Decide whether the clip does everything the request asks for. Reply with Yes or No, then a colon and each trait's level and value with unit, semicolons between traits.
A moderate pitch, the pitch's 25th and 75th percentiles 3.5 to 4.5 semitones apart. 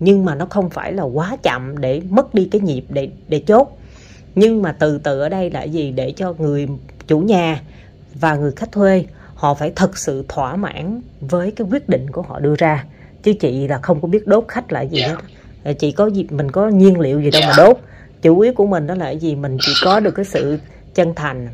No: medium, 160 Hz; average, 5.2 semitones